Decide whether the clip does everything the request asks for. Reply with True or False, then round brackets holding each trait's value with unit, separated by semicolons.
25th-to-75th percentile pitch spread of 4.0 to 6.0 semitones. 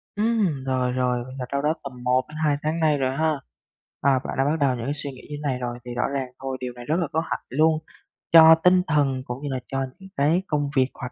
False (3.3 semitones)